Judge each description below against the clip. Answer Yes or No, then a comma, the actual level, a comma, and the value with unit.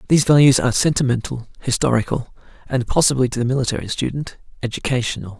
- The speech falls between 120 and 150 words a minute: Yes, slow, 135 wpm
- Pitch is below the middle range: Yes, low, 125 Hz